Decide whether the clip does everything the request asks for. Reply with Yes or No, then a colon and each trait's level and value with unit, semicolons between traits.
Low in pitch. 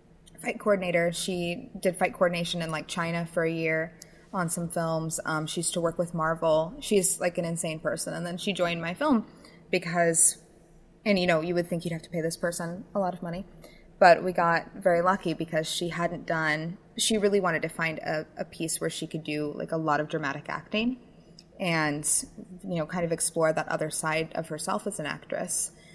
No: medium, 170 Hz